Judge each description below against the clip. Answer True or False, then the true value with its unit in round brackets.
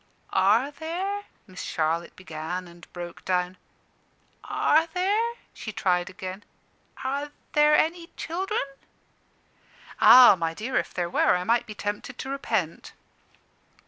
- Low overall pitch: False (215 Hz)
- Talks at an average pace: False (130 wpm)